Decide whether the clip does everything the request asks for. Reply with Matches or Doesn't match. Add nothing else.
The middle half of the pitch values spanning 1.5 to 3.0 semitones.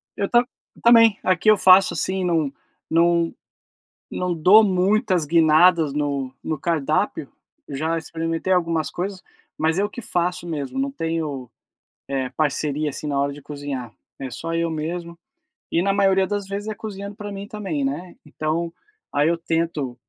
Doesn't match